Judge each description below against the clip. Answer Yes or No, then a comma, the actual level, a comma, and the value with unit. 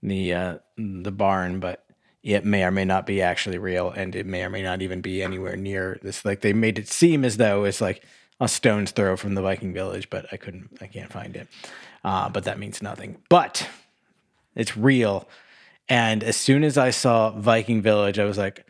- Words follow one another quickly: Yes, fast, 210 wpm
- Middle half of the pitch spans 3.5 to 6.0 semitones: No, average, 2.9 semitones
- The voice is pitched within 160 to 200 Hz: No, low, 100 Hz